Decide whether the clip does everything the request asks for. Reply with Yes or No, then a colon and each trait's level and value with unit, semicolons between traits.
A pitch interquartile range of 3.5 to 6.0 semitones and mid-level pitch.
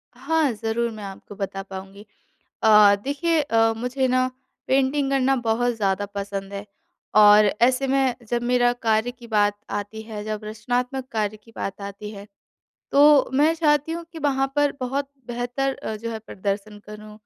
No: average, 4.3 semitones; high, 230 Hz